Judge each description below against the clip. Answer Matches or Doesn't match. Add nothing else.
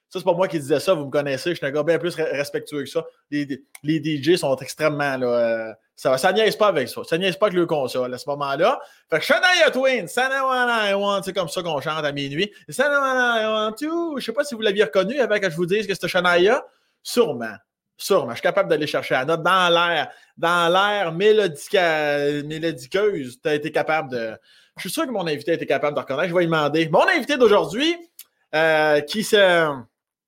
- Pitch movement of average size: Doesn't match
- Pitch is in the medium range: Matches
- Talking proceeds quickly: Matches